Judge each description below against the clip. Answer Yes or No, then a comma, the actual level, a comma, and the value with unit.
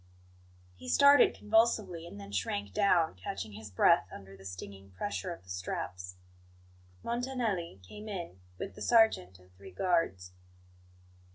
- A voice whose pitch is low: Yes, low, 100 Hz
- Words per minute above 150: No, average, 140 wpm